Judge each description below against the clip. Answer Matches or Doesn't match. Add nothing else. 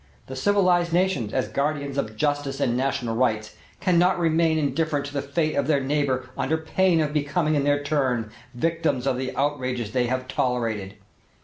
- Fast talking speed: Doesn't match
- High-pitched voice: Doesn't match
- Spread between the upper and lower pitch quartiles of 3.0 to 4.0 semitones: Matches